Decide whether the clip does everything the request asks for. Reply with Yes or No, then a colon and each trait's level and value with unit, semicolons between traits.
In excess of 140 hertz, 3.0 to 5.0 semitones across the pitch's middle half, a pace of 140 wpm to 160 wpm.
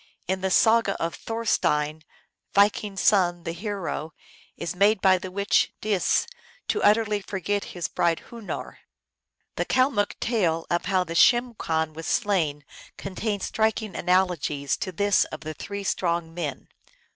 Yes: high, 190 Hz; average, 3.7 semitones; average, 145 wpm